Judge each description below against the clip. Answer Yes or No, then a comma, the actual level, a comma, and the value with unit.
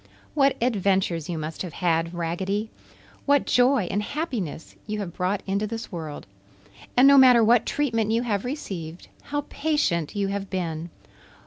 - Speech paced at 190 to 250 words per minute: No, average, 155 wpm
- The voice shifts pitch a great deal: Yes, wide, 6.0 semitones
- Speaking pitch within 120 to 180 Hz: No, high, 200 Hz